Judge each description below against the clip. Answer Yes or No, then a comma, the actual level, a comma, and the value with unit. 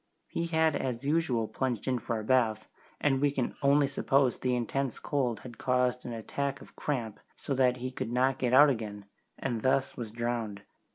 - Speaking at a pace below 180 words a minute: No, average, 190 wpm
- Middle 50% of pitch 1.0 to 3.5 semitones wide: Yes, average, 2.8 semitones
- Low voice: Yes, low, 125 Hz